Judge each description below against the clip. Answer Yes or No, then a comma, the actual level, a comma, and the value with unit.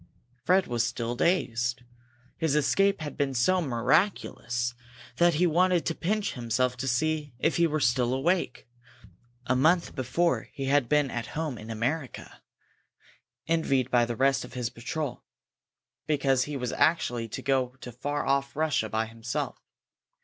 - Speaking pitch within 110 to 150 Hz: Yes, low, 135 Hz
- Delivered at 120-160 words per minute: Yes, average, 155 wpm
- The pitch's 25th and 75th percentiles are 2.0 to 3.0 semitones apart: No, average, 4.6 semitones